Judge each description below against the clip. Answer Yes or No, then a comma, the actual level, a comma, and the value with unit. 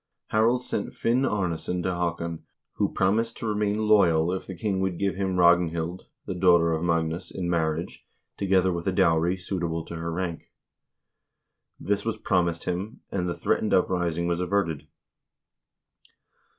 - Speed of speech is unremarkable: Yes, average, 160 wpm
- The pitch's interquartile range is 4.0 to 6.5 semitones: No, narrow, 2.6 semitones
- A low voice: Yes, very low, 90 Hz